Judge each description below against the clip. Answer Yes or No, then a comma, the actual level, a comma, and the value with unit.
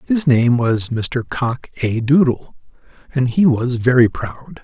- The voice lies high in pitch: No, low, 125 Hz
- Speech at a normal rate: Yes, average, 155 wpm